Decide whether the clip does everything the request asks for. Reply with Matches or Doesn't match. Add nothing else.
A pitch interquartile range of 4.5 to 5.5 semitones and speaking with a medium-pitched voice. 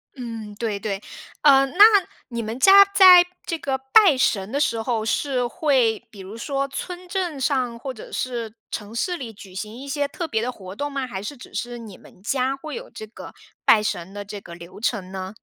Doesn't match